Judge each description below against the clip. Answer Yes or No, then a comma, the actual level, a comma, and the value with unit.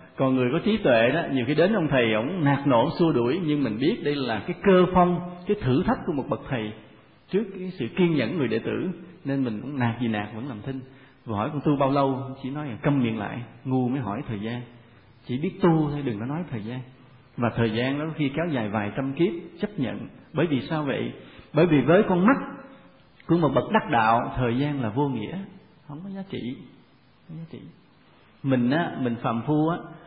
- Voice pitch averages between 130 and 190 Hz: Yes, low, 135 Hz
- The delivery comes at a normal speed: Yes, average, 235 wpm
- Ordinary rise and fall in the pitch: No, wide, 5.7 semitones